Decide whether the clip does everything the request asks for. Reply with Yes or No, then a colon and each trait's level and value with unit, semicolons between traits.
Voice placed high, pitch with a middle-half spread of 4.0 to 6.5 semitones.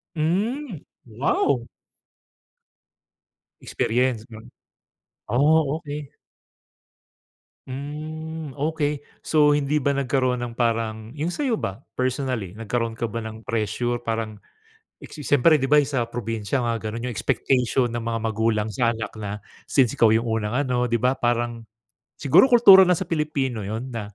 No: low, 125 Hz; average, 4.4 semitones